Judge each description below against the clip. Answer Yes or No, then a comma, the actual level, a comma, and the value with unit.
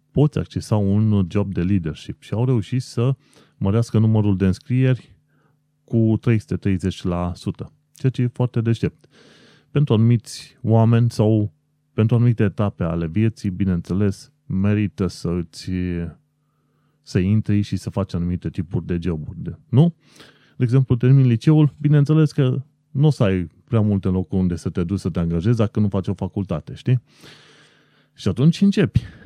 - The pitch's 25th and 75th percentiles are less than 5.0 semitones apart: No, wide, 5.6 semitones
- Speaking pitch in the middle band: No, low, 110 Hz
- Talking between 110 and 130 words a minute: No, average, 150 wpm